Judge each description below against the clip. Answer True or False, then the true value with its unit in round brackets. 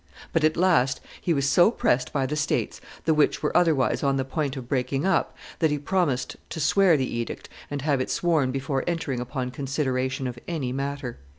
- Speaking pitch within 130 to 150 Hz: True (140 Hz)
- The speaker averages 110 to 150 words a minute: False (200 wpm)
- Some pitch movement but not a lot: True (3.2 semitones)